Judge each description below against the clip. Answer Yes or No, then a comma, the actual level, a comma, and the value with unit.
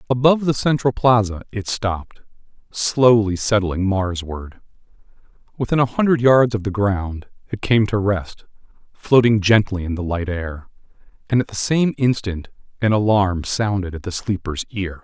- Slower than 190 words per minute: Yes, average, 150 wpm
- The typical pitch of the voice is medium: No, low, 105 Hz